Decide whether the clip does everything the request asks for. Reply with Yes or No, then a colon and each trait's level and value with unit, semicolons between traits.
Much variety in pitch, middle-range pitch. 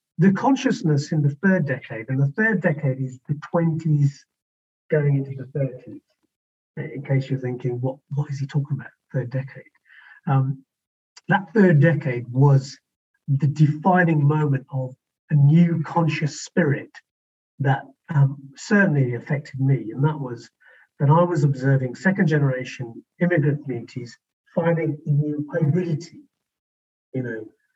No: average, 3.7 semitones; medium, 145 Hz